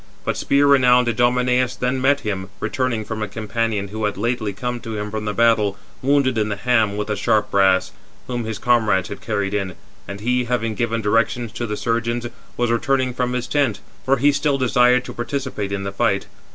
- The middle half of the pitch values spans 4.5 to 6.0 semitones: No, average, 3.1 semitones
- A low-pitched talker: Yes, low, 115 Hz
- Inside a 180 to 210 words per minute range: Yes, fast, 205 wpm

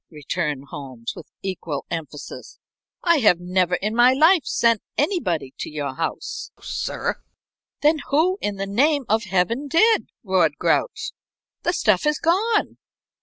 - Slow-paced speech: No, average, 145 wpm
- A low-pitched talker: No, high, 210 Hz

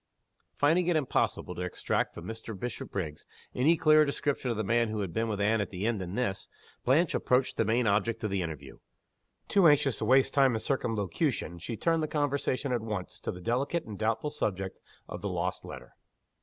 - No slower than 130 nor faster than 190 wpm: No, average, 200 wpm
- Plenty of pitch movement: Yes, wide, 5.7 semitones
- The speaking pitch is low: Yes, low, 115 Hz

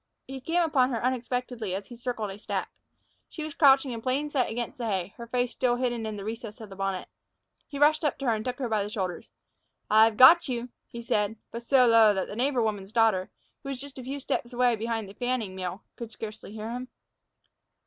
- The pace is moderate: No, fast, 230 wpm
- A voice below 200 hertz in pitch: No, high, 235 Hz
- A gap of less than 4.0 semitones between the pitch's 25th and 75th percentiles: Yes, average, 3.1 semitones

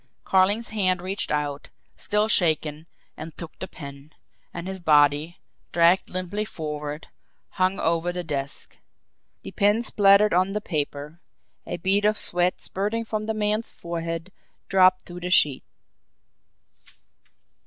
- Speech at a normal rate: No, slow, 130 wpm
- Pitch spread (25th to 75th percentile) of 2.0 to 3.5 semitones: No, average, 4.1 semitones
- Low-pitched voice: No, medium, 180 Hz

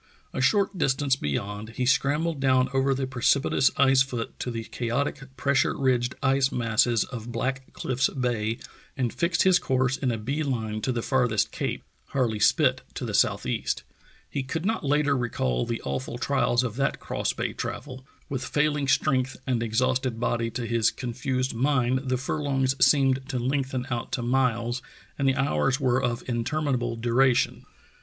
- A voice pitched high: No, low, 130 Hz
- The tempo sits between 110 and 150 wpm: No, average, 170 wpm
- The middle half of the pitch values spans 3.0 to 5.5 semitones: No, narrow, 2.4 semitones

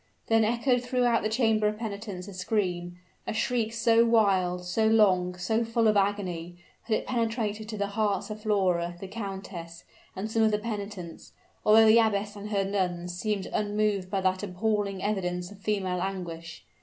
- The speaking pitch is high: Yes, high, 205 Hz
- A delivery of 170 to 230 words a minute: Yes, average, 175 wpm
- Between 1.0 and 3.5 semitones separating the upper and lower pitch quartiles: Yes, average, 3.0 semitones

